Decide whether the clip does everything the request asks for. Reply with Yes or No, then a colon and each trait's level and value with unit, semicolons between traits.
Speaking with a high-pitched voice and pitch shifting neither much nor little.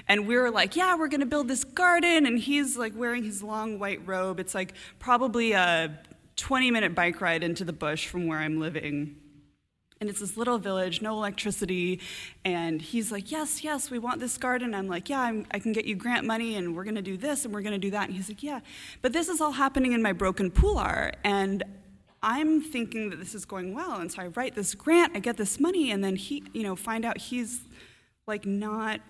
Yes: high, 215 Hz; average, 4.8 semitones